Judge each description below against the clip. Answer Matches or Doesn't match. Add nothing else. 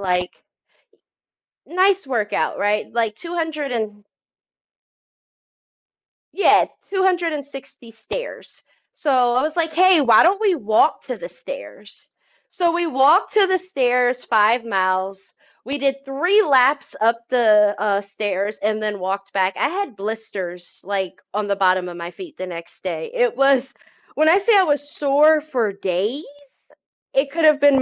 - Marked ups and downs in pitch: Matches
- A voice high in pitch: Matches